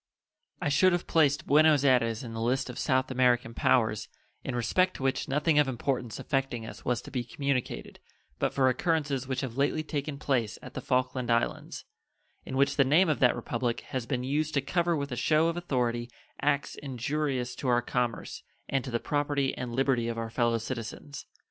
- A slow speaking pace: No, average, 195 wpm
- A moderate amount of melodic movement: Yes, average, 3.0 semitones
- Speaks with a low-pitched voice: Yes, low, 130 Hz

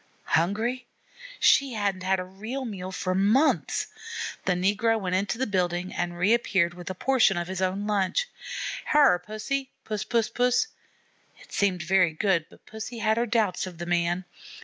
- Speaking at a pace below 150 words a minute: No, average, 170 wpm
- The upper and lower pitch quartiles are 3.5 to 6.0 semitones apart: Yes, average, 3.9 semitones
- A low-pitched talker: No, high, 195 Hz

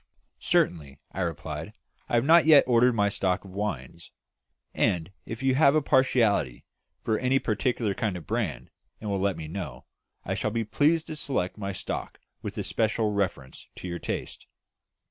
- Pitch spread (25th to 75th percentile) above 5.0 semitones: Yes, wide, 5.6 semitones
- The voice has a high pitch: No, low, 105 Hz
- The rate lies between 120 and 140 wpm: No, average, 170 wpm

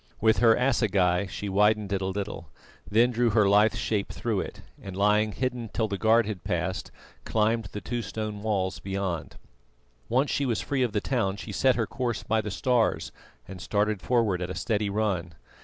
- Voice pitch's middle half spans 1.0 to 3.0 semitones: Yes, average, 2.7 semitones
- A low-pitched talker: Yes, low, 105 Hz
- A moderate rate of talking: Yes, average, 190 wpm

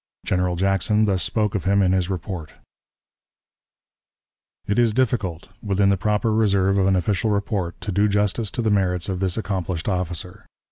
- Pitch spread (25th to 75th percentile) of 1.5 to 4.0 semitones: Yes, narrow, 2.4 semitones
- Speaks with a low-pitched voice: Yes, very low, 95 Hz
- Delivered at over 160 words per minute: Yes, average, 170 wpm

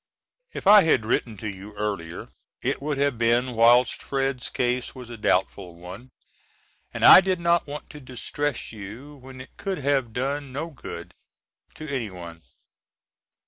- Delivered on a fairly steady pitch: No, average, 4.8 semitones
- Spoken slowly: No, average, 155 wpm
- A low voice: Yes, low, 125 Hz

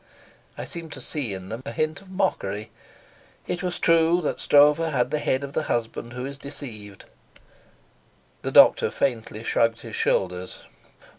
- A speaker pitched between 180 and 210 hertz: No, low, 135 Hz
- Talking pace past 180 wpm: No, average, 160 wpm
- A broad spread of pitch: Yes, wide, 5.8 semitones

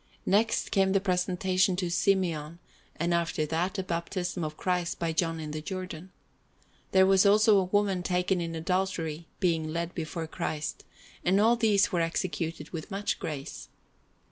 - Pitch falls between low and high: Yes, medium, 180 Hz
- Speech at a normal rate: Yes, average, 160 wpm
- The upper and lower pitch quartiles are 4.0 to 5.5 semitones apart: No, average, 2.7 semitones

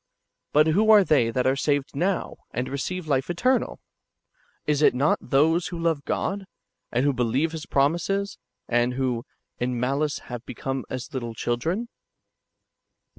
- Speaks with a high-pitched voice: No, medium, 140 Hz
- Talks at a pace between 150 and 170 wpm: Yes, average, 160 wpm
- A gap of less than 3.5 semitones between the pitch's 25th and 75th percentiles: No, average, 4.9 semitones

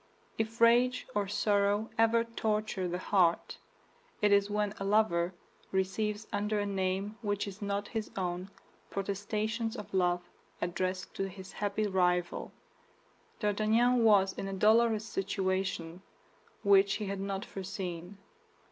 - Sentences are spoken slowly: Yes, slow, 130 wpm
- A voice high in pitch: Yes, high, 200 Hz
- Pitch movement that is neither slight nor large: No, narrow, 2.2 semitones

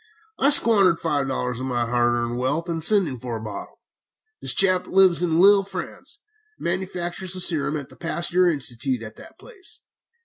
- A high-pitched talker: No, medium, 165 Hz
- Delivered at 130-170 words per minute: No, average, 180 wpm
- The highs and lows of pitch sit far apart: Yes, wide, 6.6 semitones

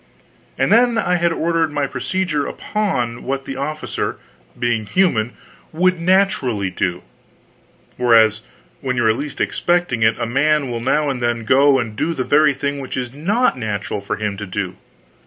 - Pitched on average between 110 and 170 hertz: Yes, low, 135 Hz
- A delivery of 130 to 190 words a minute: Yes, average, 170 wpm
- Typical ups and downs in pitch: No, wide, 5.9 semitones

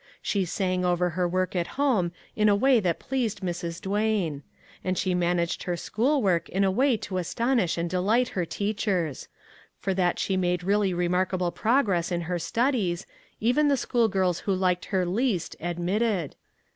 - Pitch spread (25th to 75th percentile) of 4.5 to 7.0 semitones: No, average, 3.5 semitones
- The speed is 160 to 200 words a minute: Yes, average, 170 wpm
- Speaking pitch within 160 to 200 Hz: Yes, medium, 185 Hz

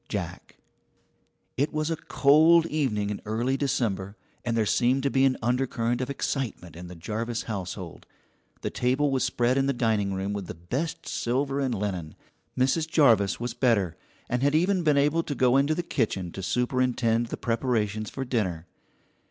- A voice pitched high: No, low, 125 Hz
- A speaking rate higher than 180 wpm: No, average, 175 wpm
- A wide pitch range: No, average, 4.7 semitones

